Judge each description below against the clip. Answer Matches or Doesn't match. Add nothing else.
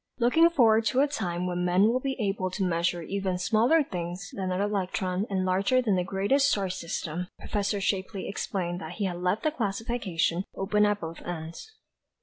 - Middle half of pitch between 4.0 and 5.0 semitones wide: Doesn't match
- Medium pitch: Doesn't match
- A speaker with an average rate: Matches